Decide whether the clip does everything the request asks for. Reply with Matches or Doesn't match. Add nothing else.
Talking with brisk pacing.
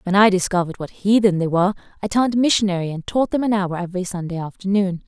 Matches